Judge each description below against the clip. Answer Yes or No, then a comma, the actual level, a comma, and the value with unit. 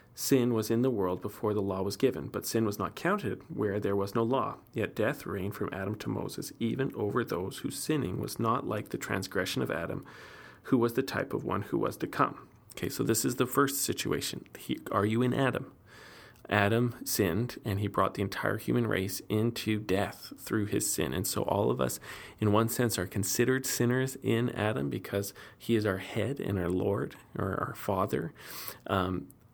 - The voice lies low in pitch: Yes, low, 105 Hz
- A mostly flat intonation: No, average, 3.6 semitones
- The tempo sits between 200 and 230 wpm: Yes, fast, 205 wpm